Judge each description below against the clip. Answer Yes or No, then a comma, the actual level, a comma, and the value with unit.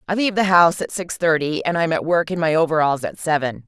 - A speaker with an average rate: No, fast, 260 wpm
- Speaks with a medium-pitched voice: Yes, medium, 165 Hz